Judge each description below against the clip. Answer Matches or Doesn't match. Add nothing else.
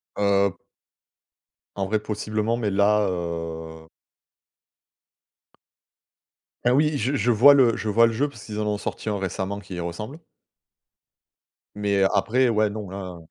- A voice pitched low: Matches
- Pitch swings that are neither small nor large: Matches